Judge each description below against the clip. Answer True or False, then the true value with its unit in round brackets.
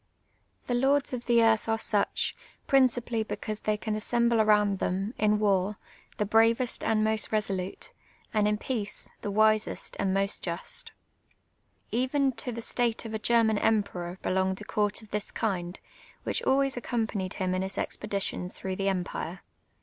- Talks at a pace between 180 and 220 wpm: False (165 wpm)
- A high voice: True (215 Hz)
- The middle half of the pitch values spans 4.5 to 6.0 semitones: False (2.9 semitones)